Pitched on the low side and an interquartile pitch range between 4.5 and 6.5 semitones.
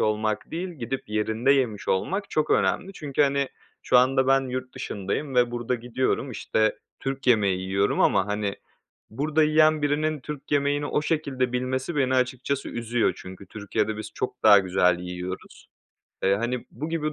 Yes: low, 125 Hz; average, 4.9 semitones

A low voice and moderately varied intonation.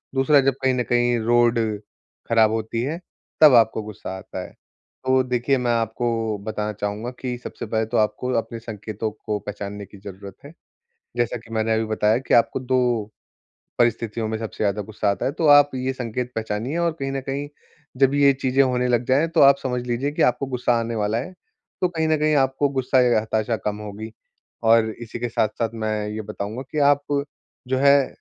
Yes: low, 120 Hz; average, 3.3 semitones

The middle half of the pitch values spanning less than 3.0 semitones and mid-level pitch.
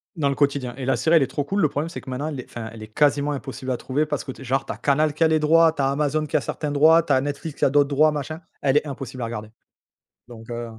Yes: narrow, 2.6 semitones; medium, 145 Hz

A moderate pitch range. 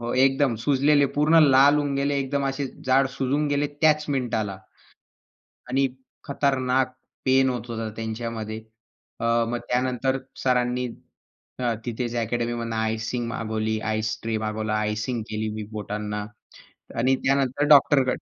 Yes: average, 3.5 semitones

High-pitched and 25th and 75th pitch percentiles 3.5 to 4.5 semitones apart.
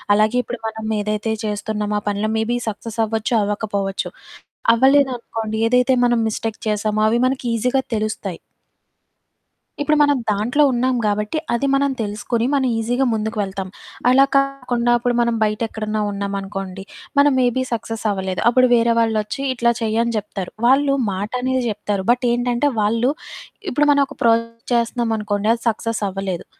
No: high, 225 Hz; average, 2.8 semitones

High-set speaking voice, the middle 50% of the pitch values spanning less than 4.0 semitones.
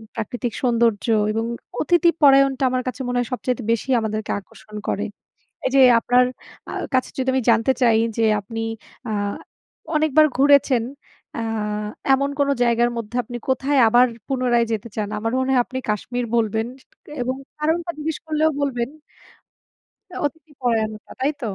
Yes: very high, 250 Hz; average, 3.2 semitones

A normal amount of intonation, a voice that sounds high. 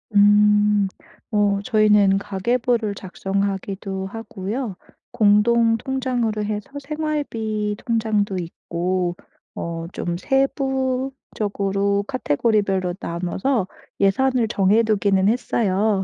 Yes: average, 3.2 semitones; high, 210 Hz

